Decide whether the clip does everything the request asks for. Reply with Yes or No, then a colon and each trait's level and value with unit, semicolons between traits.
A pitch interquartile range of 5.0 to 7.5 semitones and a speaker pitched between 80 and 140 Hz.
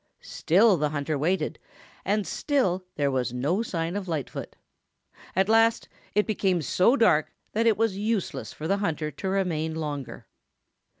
No: average, 5.3 semitones; medium, 180 Hz